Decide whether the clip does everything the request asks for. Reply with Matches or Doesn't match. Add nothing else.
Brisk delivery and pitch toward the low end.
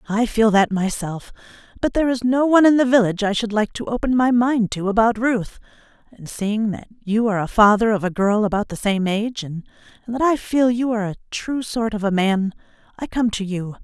Doesn't match